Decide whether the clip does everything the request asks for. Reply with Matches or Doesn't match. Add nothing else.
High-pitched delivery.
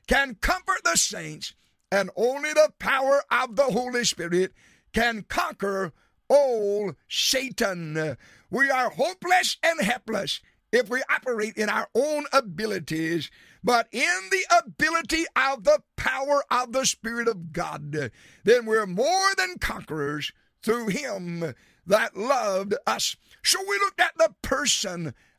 Matches